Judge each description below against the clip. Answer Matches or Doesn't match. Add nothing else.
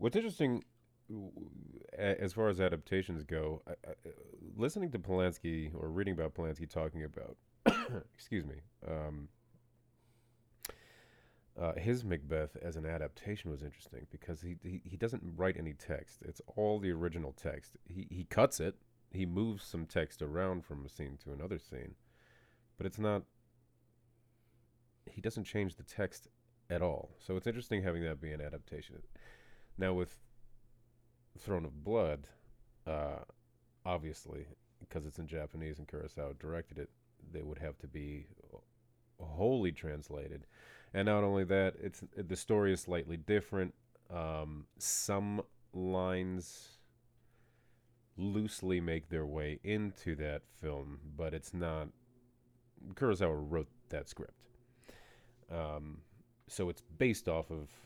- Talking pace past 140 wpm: Doesn't match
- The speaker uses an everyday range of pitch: Doesn't match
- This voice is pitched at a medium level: Doesn't match